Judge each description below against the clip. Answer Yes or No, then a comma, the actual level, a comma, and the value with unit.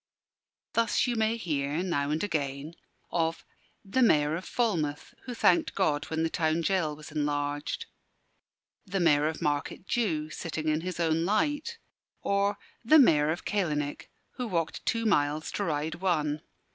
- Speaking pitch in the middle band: Yes, medium, 165 Hz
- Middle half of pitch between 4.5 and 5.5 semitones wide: Yes, average, 4.9 semitones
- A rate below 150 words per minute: No, average, 155 wpm